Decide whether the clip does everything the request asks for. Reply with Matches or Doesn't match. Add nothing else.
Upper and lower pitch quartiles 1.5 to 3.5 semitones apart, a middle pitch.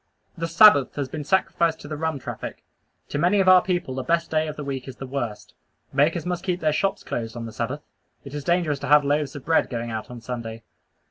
Doesn't match